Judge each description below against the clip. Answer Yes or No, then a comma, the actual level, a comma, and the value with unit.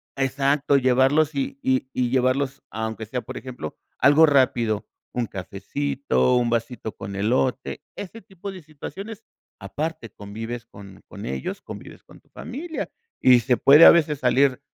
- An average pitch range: Yes, average, 3.8 semitones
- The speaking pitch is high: No, low, 130 Hz